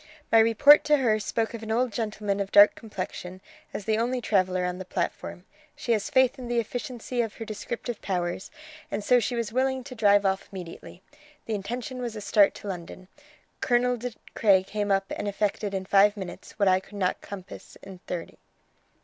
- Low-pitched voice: No, high, 210 Hz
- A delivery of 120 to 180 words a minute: No, average, 195 wpm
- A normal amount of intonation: Yes, average, 3.6 semitones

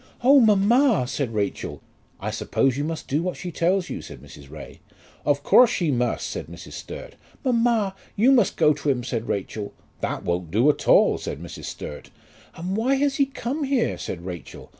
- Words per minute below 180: No, average, 190 wpm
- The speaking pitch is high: No, medium, 170 Hz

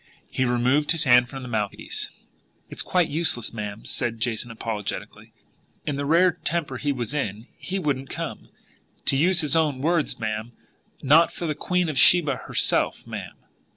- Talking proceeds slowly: No, average, 165 wpm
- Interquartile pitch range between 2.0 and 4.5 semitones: No, average, 5.1 semitones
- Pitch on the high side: No, low, 135 Hz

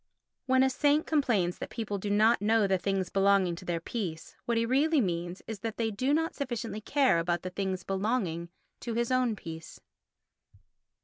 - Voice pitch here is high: Yes, high, 210 Hz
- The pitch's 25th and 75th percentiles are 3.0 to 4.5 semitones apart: No, average, 5.3 semitones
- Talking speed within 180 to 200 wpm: Yes, average, 185 wpm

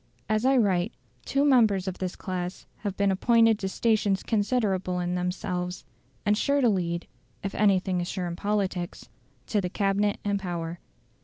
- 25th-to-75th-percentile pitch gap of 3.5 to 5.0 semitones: No, average, 2.9 semitones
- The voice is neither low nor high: No, high, 195 Hz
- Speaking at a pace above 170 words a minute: No, average, 165 wpm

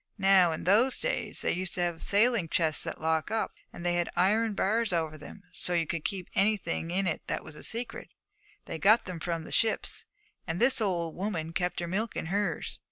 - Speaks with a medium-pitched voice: Yes, medium, 180 Hz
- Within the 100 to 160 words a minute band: No, fast, 205 wpm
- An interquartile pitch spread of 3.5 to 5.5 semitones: Yes, average, 4.1 semitones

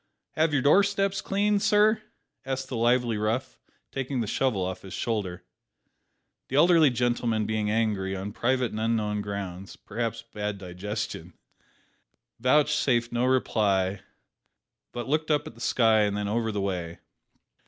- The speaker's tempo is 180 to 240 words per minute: No, average, 145 wpm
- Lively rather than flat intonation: No, average, 4.4 semitones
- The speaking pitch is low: Yes, low, 115 Hz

